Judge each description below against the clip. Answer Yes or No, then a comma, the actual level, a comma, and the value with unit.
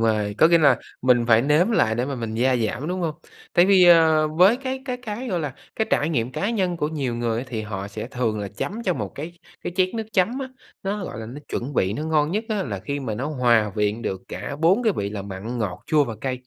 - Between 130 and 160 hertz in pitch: Yes, medium, 140 Hz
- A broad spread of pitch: Yes, wide, 8.0 semitones